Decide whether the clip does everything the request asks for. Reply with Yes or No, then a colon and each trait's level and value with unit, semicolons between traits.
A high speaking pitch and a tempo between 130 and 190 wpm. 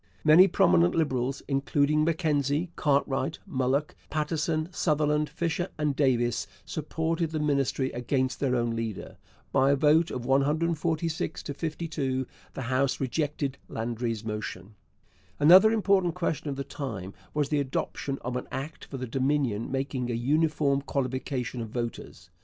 No: medium, 140 Hz; average, 140 wpm